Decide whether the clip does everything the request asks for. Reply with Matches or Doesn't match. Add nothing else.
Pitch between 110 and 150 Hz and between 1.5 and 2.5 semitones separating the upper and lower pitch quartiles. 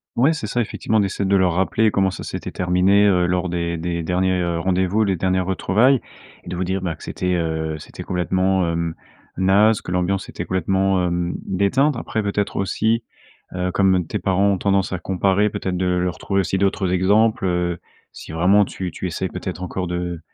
Doesn't match